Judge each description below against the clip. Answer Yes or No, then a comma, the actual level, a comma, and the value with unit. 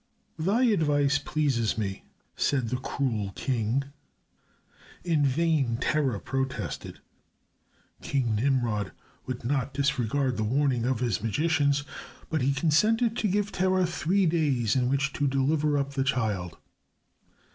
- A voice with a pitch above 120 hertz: Yes, medium, 140 Hz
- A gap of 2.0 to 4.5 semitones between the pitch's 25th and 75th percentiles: Yes, average, 4.1 semitones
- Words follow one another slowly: Yes, slow, 125 wpm